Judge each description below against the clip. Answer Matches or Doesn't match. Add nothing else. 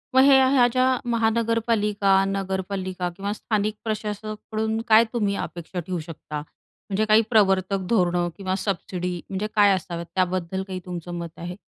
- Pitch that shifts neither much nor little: Matches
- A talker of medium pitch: Doesn't match